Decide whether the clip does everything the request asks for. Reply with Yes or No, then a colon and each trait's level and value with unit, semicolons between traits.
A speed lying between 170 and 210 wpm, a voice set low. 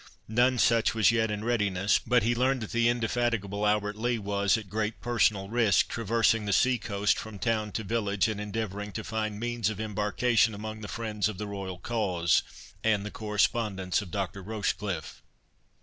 Yes: average, 180 wpm; low, 110 Hz